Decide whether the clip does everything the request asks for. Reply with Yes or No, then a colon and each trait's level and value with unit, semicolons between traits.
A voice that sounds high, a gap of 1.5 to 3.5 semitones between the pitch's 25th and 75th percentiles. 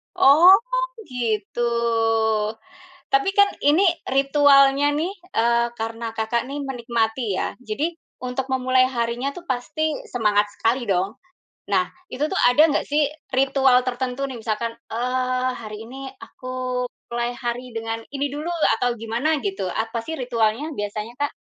Yes: very high, 250 Hz; average, 3.2 semitones